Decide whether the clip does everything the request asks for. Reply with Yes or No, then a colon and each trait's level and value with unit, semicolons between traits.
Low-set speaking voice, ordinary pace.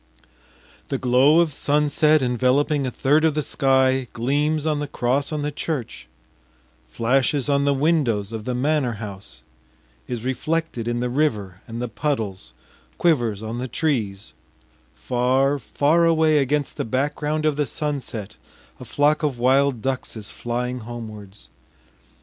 Yes: low, 130 Hz; average, 145 wpm